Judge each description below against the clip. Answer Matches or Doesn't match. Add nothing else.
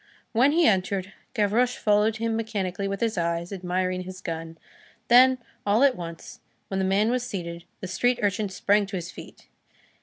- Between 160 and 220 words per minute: Matches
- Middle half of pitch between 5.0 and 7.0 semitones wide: Doesn't match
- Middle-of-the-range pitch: Doesn't match